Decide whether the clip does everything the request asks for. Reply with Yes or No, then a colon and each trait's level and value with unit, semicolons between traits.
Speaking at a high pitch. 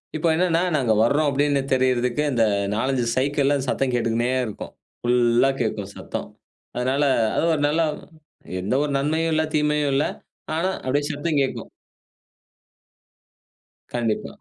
No: low, 135 Hz